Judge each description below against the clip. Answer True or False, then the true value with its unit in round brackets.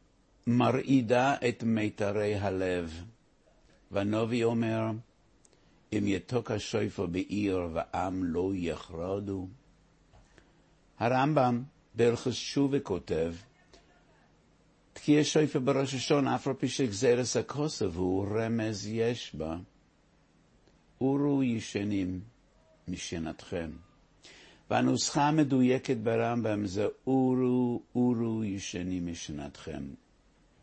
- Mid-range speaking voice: False (115 Hz)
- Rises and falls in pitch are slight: False (4.7 semitones)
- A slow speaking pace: True (80 wpm)